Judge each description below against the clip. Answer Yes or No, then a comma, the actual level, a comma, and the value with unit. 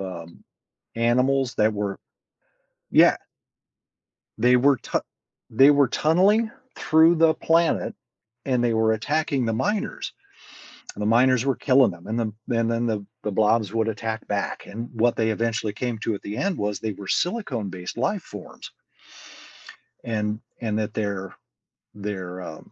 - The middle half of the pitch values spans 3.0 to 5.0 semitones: Yes, average, 4.1 semitones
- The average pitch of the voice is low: Yes, low, 115 Hz